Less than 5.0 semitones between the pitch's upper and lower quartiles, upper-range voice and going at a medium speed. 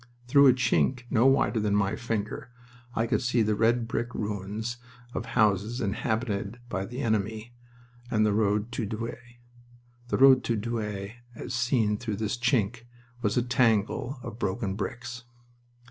No: narrow, 2.5 semitones; low, 115 Hz; average, 160 wpm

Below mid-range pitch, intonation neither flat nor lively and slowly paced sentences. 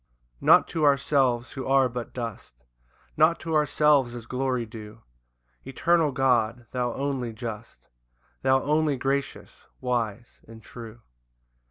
Yes: low, 125 Hz; average, 3.0 semitones; slow, 130 wpm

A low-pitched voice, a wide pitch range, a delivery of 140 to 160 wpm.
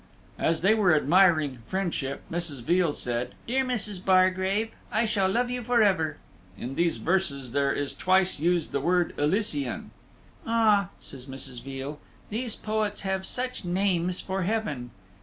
No: medium, 185 Hz; wide, 6.0 semitones; average, 145 wpm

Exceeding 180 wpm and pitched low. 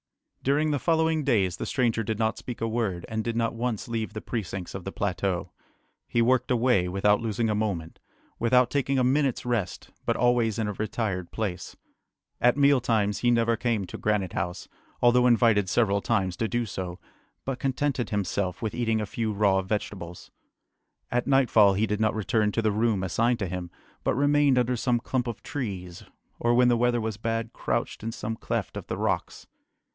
Yes: average, 190 wpm; low, 115 Hz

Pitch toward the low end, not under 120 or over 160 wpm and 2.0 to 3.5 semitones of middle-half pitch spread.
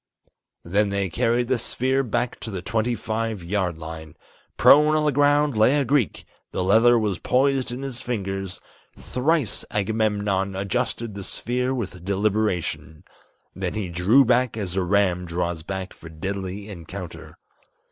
No: low, 105 Hz; average, 150 wpm; average, 4.7 semitones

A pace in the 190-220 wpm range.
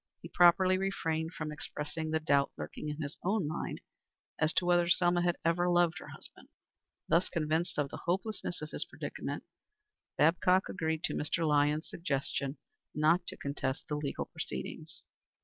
No: average, 160 wpm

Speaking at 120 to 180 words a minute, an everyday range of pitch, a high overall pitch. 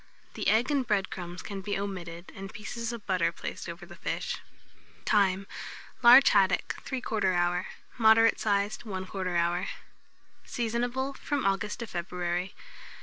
Yes: average, 140 wpm; average, 3.7 semitones; high, 200 Hz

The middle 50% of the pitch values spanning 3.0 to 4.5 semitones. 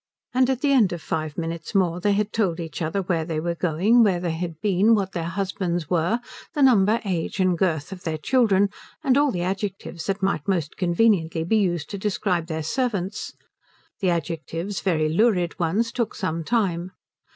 Yes: average, 3.8 semitones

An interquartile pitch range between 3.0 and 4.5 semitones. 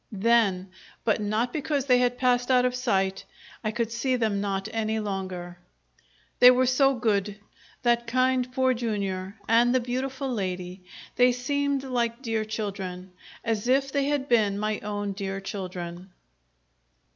Yes: average, 4.1 semitones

